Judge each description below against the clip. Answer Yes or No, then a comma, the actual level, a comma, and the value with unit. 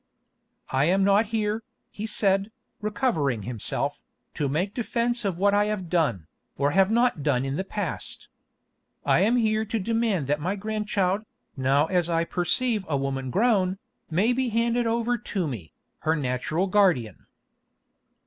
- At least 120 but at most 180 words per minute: Yes, average, 155 wpm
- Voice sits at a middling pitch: No, high, 195 Hz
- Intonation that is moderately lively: No, wide, 6.5 semitones